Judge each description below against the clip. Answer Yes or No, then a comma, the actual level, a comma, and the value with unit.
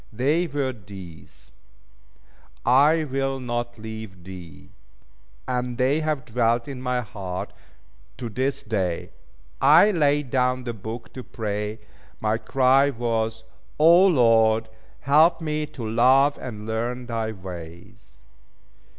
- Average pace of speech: No, slow, 120 wpm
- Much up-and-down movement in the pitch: No, average, 3.7 semitones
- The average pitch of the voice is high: No, low, 120 Hz